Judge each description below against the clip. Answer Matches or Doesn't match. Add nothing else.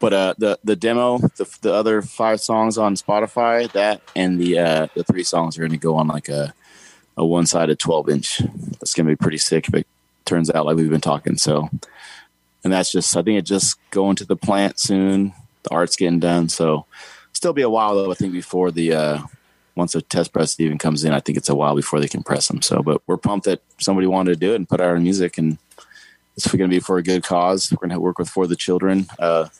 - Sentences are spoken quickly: Matches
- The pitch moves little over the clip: Doesn't match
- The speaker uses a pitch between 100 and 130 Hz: Doesn't match